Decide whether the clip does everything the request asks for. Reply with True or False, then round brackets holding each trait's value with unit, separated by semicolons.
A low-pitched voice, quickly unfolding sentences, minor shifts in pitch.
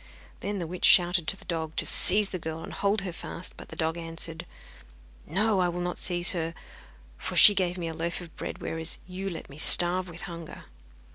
False (175 Hz; 215 wpm; 2.1 semitones)